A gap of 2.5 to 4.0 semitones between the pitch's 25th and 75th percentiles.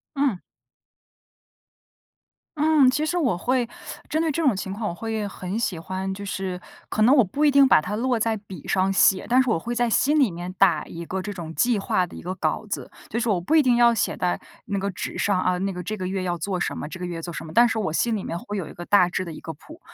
No: average, 4.9 semitones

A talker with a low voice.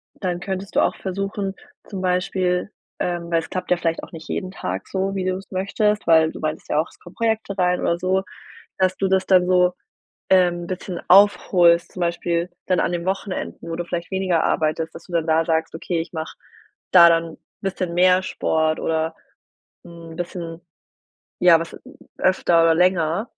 No: medium, 180 Hz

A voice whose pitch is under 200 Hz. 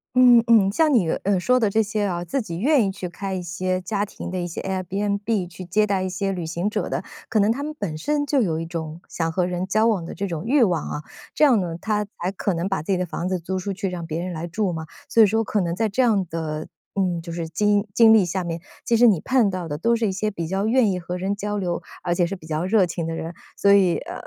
Yes: high, 190 Hz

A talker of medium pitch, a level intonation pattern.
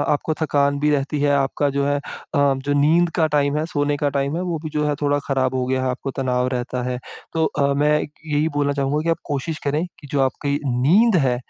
Yes: medium, 145 Hz; narrow, 1.7 semitones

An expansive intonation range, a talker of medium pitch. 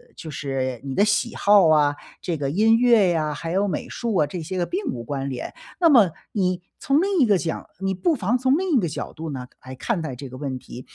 Yes: wide, 7.8 semitones; medium, 175 Hz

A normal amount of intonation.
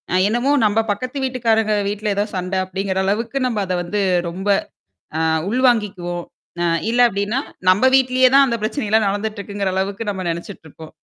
Yes: average, 3.5 semitones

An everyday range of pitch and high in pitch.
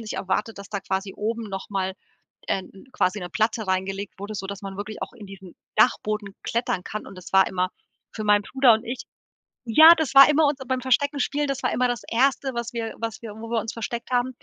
Yes: average, 4.1 semitones; high, 220 Hz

